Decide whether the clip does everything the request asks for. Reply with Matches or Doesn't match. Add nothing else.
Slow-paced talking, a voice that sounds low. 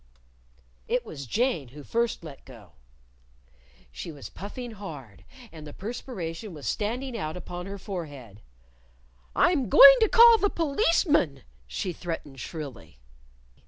Doesn't match